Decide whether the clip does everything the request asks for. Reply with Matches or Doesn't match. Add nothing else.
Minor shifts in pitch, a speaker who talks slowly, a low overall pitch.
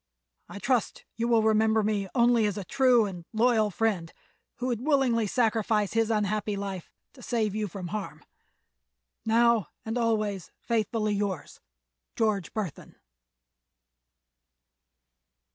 Doesn't match